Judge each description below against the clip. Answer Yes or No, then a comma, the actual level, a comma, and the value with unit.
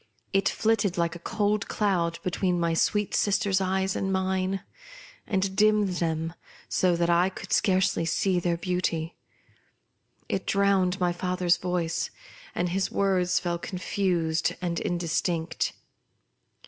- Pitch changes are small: Yes, narrow, 2.1 semitones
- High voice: No, medium, 180 Hz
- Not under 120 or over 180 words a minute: Yes, slow, 135 wpm